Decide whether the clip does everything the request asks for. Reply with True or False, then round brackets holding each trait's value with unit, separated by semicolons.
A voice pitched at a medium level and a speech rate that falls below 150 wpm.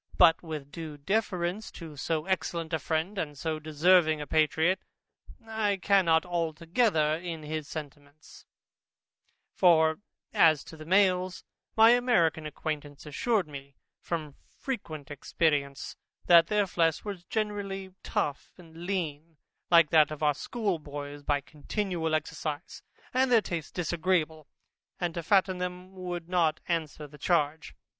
True (165 Hz; 135 wpm)